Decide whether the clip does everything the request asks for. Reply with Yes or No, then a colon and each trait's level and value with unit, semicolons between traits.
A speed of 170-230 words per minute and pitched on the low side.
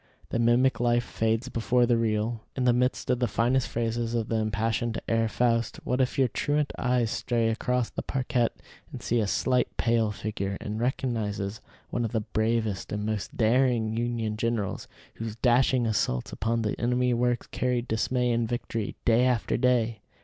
Yes: average, 175 wpm; low, 115 Hz